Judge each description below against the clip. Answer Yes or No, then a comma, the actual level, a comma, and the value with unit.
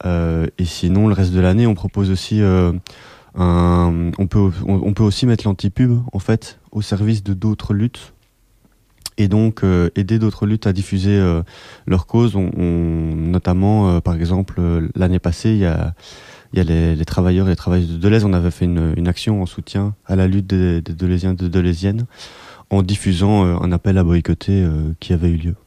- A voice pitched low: Yes, very low, 95 Hz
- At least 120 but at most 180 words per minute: No, average, 205 wpm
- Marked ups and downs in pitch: No, average, 2.8 semitones